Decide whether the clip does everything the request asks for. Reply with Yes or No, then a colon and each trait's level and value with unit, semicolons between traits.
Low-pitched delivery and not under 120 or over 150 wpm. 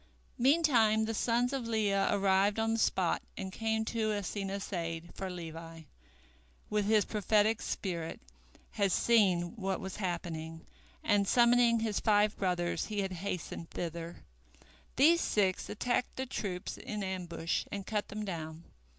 No: high, 200 Hz; average, 140 wpm